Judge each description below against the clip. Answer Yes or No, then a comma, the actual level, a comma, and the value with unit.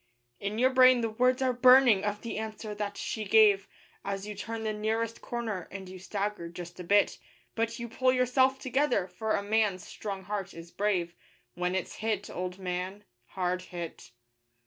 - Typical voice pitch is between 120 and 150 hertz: No, high, 210 Hz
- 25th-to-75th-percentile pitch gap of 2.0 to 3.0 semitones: No, average, 3.5 semitones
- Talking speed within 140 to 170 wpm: No, average, 180 wpm